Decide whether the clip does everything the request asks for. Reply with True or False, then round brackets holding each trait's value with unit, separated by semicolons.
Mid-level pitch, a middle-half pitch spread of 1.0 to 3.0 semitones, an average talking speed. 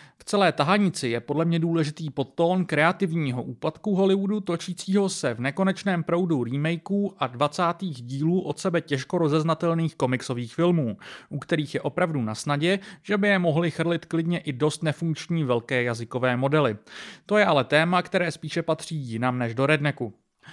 False (160 Hz; 4.1 semitones; 160 wpm)